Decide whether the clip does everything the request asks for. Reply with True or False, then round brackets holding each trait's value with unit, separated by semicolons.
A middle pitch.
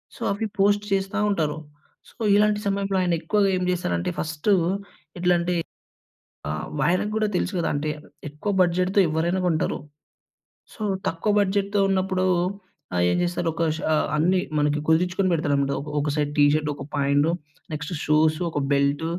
True (170 Hz)